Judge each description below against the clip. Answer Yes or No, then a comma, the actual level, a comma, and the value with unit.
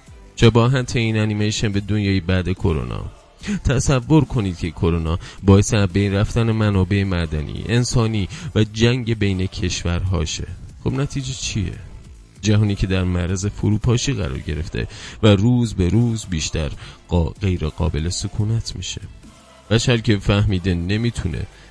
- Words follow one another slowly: No, average, 125 wpm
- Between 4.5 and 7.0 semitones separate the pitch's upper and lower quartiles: No, average, 3.8 semitones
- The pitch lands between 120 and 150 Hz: No, low, 100 Hz